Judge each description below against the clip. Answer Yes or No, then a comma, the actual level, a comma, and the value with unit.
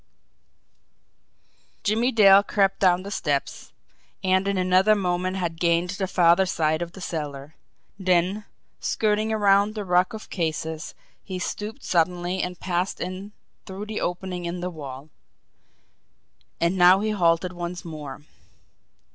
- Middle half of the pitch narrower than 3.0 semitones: Yes, narrow, 2.5 semitones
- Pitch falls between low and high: Yes, medium, 180 Hz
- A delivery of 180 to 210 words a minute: No, slow, 135 wpm